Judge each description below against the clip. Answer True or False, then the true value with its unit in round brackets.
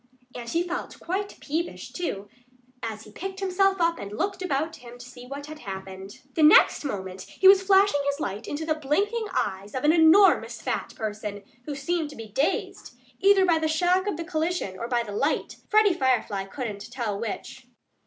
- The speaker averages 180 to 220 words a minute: True (195 wpm)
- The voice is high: True (295 Hz)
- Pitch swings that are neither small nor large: False (8.3 semitones)